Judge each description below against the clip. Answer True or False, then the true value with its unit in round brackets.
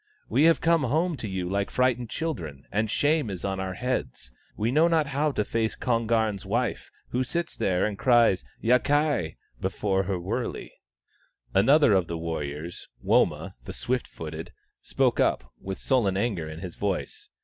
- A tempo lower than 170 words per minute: False (175 wpm)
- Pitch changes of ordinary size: False (6.0 semitones)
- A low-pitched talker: True (110 Hz)